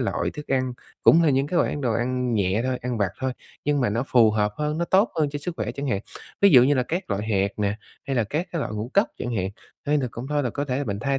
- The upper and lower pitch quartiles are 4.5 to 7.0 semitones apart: Yes, average, 4.9 semitones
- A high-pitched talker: No, low, 130 Hz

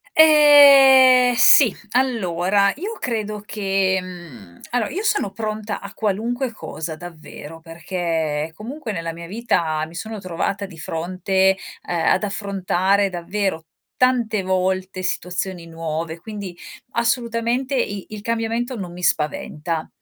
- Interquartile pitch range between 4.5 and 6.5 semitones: Yes, average, 5.1 semitones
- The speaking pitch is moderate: No, high, 195 Hz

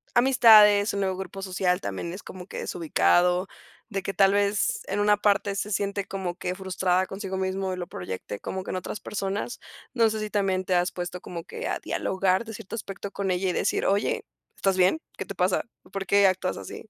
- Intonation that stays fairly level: Yes, narrow, 1.8 semitones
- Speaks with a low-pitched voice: No, high, 195 Hz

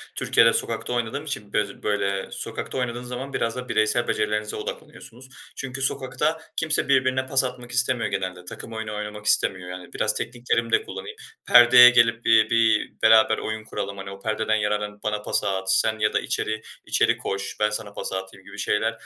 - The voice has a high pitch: No, low, 110 Hz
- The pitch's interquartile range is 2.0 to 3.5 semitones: Yes, average, 2.9 semitones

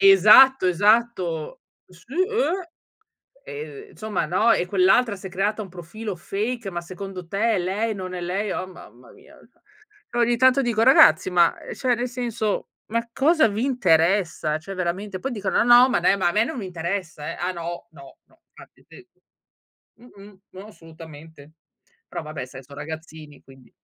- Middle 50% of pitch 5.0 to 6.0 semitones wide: Yes, average, 5.3 semitones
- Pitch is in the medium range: No, high, 195 Hz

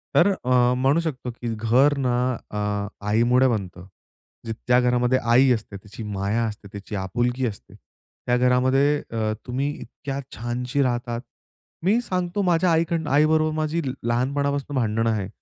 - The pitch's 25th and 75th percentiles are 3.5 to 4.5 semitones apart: Yes, average, 3.9 semitones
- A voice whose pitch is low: Yes, low, 125 Hz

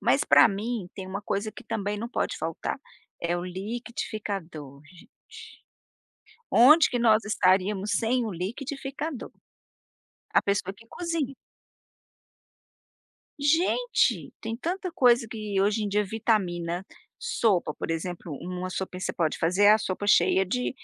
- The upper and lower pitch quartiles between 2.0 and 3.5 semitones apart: No, average, 4.7 semitones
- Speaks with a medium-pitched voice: No, high, 210 Hz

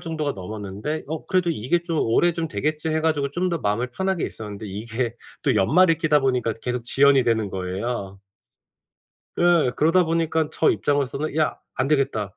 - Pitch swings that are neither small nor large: No, wide, 6.2 semitones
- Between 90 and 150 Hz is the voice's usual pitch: Yes, medium, 140 Hz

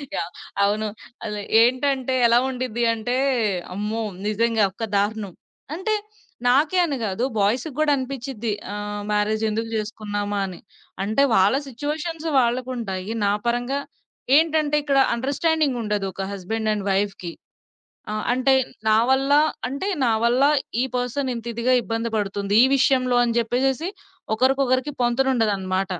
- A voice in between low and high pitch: No, high, 235 Hz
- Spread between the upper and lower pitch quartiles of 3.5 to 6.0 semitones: Yes, average, 4.1 semitones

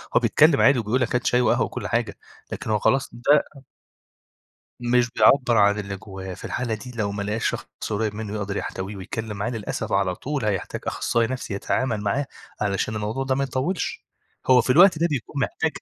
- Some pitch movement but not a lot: Yes, average, 4.1 semitones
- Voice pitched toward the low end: Yes, low, 115 Hz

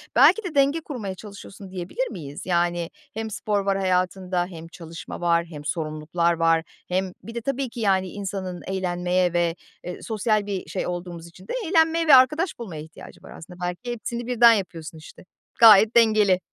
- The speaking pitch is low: No, high, 190 Hz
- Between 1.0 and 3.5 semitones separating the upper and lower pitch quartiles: No, average, 4.9 semitones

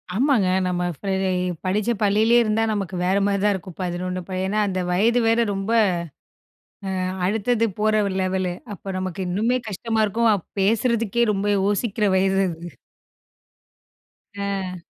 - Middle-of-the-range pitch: No, high, 200 Hz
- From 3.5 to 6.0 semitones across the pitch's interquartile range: No, average, 3.0 semitones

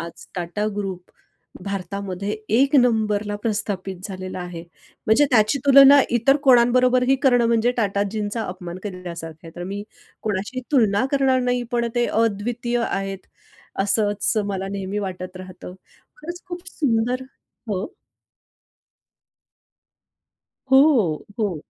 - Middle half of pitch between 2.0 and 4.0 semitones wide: No, average, 4.4 semitones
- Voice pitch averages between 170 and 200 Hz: No, high, 210 Hz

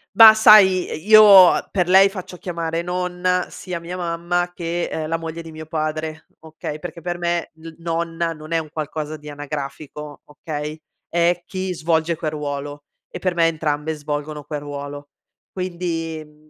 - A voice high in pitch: No, medium, 165 Hz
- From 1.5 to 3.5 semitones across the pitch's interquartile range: Yes, narrow, 2.5 semitones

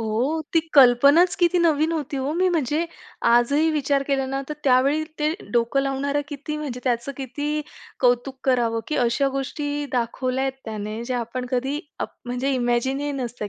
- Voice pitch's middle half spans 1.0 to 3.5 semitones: Yes, average, 3.2 semitones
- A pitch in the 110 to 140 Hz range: No, very high, 270 Hz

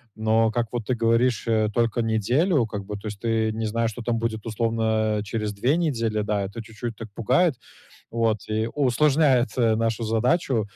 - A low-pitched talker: Yes, low, 115 Hz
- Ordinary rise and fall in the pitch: No, narrow, 1.7 semitones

